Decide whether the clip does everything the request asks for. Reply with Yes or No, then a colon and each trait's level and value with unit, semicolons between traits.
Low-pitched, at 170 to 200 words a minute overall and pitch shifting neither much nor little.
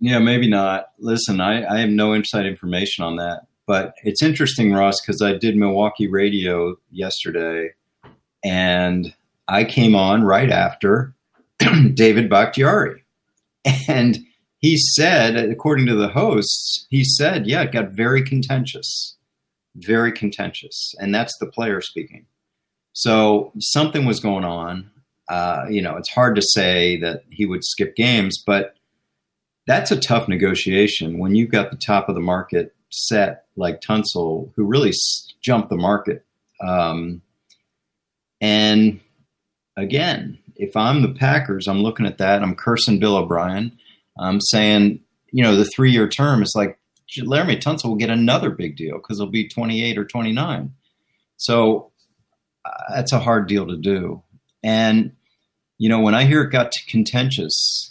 No: low, 105 Hz; average, 150 wpm; average, 3.1 semitones